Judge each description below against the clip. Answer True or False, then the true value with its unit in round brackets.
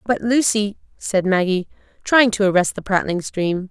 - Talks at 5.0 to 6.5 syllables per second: False (4.6 syllables/s)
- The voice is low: False (200 Hz)